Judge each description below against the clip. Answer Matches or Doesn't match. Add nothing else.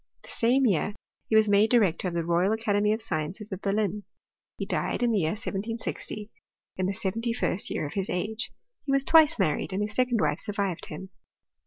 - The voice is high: Matches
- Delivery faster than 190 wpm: Matches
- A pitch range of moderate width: Matches